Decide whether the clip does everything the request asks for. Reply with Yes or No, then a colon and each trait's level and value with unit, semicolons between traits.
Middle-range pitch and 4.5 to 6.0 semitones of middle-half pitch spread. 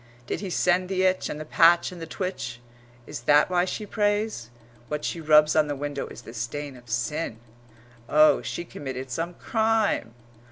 Yes: medium, 155 Hz; wide, 5.6 semitones